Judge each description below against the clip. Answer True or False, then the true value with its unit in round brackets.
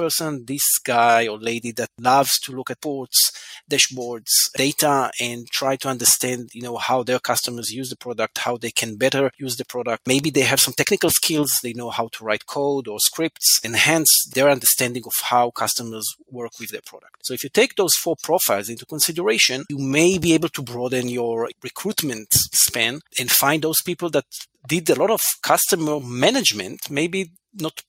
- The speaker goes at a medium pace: True (185 wpm)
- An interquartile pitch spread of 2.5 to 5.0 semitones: True (3.6 semitones)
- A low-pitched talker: True (130 Hz)